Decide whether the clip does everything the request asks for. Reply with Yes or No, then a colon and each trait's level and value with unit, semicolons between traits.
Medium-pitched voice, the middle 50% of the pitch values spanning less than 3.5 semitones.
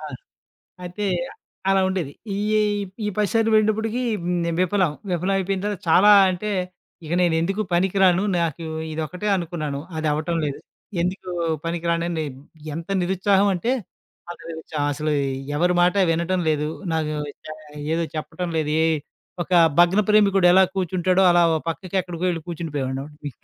Yes: medium, 175 Hz; average, 3.1 semitones